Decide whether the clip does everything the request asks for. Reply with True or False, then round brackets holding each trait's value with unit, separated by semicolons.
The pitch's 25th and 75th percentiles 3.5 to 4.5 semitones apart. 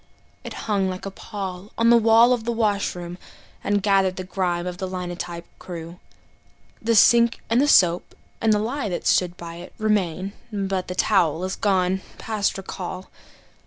False (3.1 semitones)